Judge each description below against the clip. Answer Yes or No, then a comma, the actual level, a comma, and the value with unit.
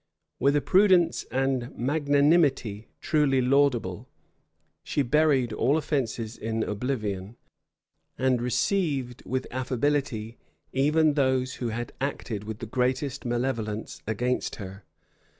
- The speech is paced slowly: Yes, slow, 110 wpm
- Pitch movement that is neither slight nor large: Yes, average, 3.8 semitones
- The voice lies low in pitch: Yes, low, 130 Hz